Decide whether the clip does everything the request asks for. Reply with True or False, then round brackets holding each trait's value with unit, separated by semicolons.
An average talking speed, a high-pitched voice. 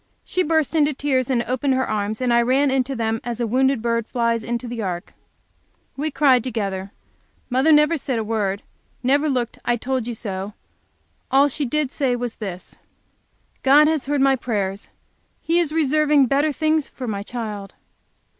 True (170 wpm; 255 Hz)